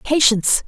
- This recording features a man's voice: No, female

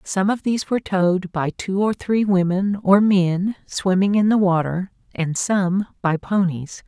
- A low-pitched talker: No, high, 190 Hz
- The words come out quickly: No, average, 175 wpm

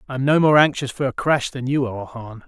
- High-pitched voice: No, low, 130 Hz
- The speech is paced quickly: Yes, fast, 290 wpm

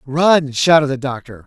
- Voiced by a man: Yes, male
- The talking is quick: No, average, 165 wpm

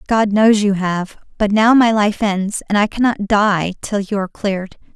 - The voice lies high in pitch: Yes, high, 205 Hz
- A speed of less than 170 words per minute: No, fast, 205 wpm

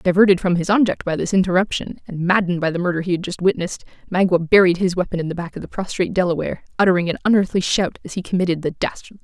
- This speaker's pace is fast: Yes, fast, 240 wpm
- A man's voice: No, female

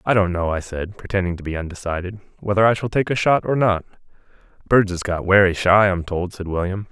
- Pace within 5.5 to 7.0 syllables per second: Yes, 5.9 syllables/s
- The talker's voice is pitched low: Yes, very low, 95 Hz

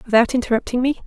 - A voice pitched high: Yes, high, 245 Hz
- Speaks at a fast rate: No, average, 170 wpm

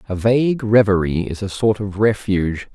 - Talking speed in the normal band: Yes, average, 175 wpm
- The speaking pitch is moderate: No, low, 105 Hz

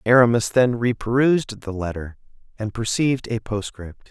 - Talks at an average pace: No, slow, 130 wpm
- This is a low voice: Yes, low, 115 Hz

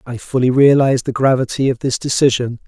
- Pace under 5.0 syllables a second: No, 6.0 syllables/s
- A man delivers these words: Yes, male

